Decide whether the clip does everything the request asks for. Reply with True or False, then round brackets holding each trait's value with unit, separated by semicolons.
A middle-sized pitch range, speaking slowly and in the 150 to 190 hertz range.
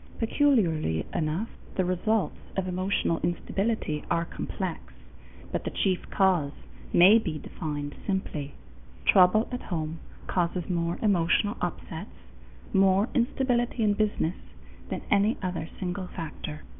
True (4.0 semitones; 120 wpm; 185 Hz)